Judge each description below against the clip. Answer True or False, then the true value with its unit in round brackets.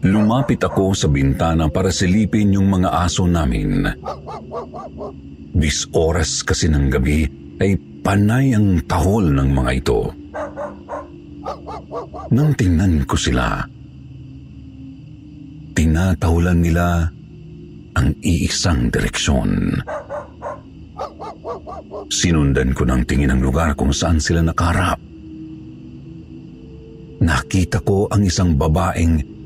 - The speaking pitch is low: True (85 Hz)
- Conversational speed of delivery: False (95 wpm)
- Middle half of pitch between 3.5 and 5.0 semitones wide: False (5.5 semitones)